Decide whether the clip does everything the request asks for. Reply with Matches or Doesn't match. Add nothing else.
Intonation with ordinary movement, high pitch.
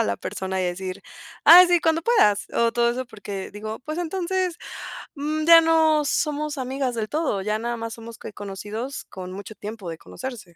Doesn't match